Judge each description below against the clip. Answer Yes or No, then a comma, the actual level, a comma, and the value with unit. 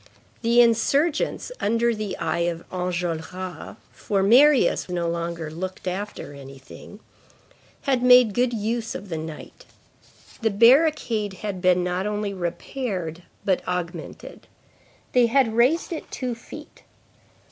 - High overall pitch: Yes, high, 205 Hz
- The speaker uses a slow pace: Yes, slow, 125 wpm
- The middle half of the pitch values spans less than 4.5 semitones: No, average, 5.1 semitones